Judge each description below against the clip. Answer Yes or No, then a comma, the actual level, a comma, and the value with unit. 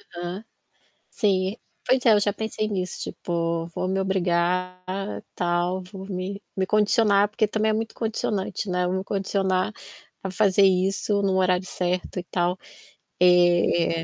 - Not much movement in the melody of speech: Yes, narrow, 2.1 semitones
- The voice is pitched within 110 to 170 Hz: No, high, 190 Hz